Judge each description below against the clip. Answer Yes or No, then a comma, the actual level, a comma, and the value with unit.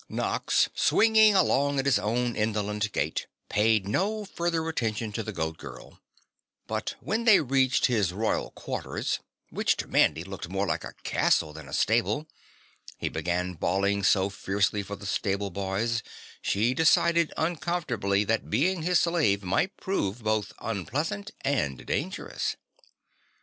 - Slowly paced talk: No, average, 145 wpm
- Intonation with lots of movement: Yes, wide, 8.1 semitones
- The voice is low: Yes, low, 110 Hz